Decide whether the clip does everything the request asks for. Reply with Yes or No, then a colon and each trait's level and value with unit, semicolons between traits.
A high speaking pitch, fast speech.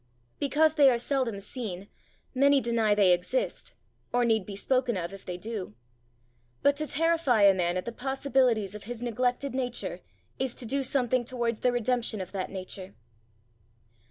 No: high, 240 Hz; average, 165 wpm